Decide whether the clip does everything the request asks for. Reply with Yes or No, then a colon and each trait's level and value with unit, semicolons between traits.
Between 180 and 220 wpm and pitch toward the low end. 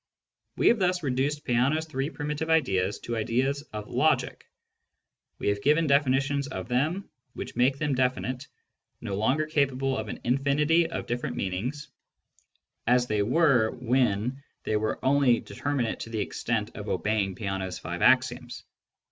No: average, 150 wpm; low, 130 Hz